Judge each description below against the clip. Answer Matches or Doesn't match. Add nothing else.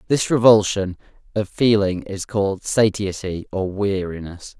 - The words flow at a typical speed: Doesn't match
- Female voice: Doesn't match